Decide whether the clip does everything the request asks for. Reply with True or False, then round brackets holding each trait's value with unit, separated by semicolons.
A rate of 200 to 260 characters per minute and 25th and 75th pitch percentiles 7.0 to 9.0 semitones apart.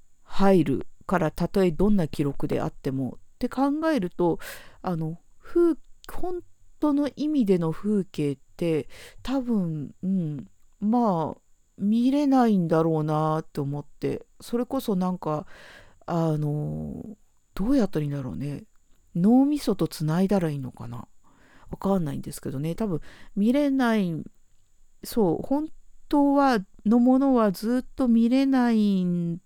True (255 characters per minute; 8.0 semitones)